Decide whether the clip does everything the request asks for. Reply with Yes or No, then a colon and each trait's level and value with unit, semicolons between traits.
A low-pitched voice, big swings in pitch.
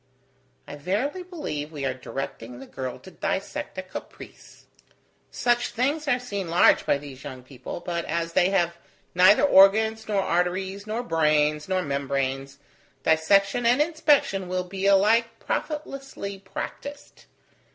No: high, 190 Hz; wide, 7.4 semitones